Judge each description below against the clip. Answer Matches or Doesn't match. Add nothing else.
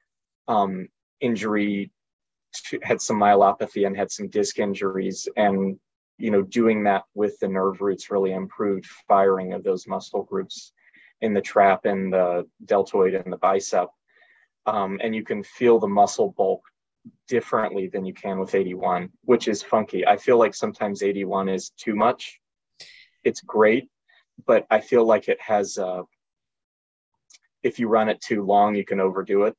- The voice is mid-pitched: Doesn't match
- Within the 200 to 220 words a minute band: Doesn't match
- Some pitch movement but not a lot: Doesn't match